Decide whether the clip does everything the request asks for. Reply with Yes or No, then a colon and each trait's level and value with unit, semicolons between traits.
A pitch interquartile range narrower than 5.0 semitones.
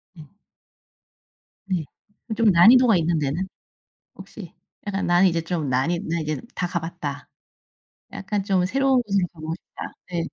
Yes: average, 3.4 semitones